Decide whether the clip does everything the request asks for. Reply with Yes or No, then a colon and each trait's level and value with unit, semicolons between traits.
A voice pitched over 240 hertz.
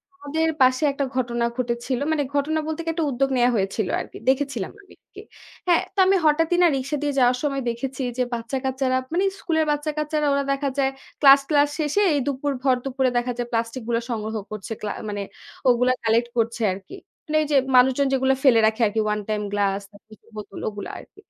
Yes: very high, 260 Hz